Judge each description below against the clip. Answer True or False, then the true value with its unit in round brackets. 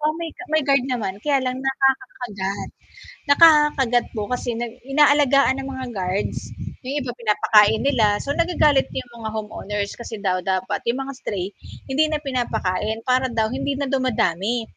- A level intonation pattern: False (4.6 semitones)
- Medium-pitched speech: False (250 Hz)